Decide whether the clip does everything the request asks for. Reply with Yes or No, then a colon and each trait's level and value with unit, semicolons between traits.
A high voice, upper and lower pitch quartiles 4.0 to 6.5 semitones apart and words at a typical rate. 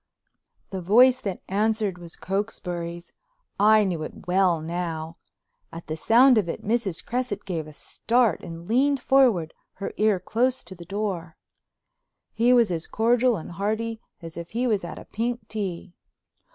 Yes: high, 200 Hz; average, 5.0 semitones; average, 160 wpm